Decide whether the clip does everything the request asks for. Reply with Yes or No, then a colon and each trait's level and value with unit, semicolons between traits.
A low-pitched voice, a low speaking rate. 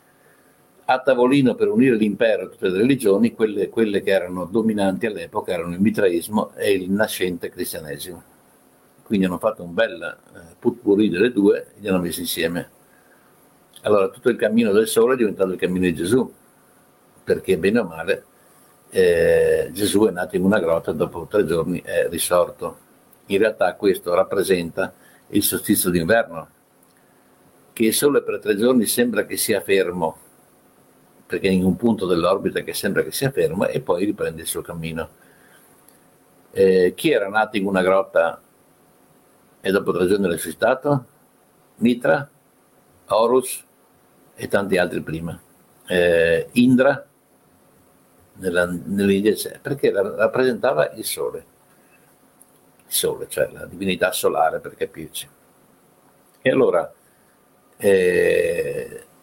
No: low, 110 Hz; average, 135 wpm